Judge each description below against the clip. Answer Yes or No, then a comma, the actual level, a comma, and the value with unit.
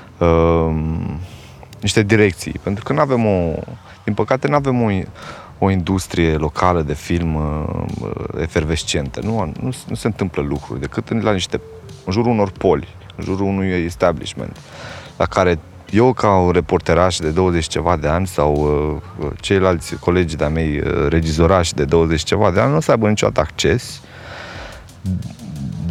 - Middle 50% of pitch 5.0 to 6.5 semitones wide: No, average, 4.1 semitones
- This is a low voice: Yes, very low, 90 Hz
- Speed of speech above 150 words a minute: Yes, average, 160 wpm